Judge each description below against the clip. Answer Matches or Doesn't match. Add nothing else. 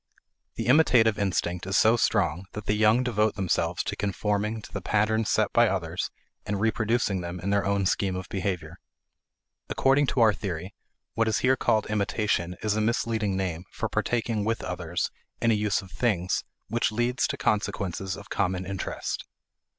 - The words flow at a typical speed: Matches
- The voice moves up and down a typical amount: Matches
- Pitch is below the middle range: Matches